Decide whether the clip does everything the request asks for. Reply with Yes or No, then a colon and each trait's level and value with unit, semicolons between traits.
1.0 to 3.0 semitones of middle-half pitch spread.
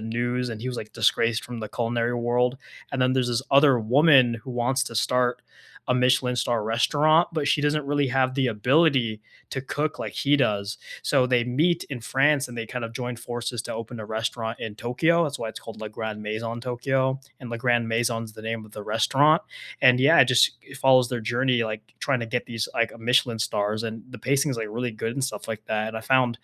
Yes: narrow, 2.6 semitones